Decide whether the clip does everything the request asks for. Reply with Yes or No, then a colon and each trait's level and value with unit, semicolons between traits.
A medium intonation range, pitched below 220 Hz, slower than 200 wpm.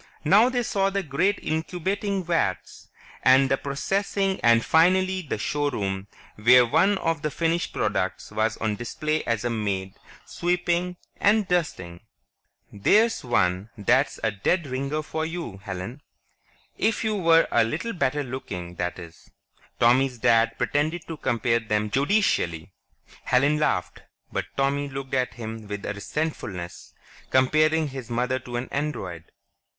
No: wide, 7.0 semitones; low, 135 Hz; average, 140 wpm